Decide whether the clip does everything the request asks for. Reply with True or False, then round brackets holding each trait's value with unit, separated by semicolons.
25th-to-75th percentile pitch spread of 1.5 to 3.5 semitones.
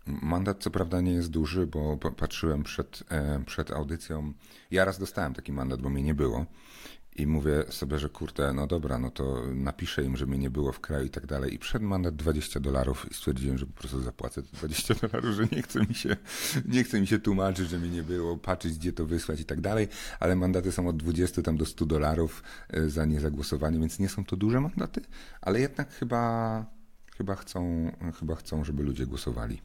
False (4.3 semitones)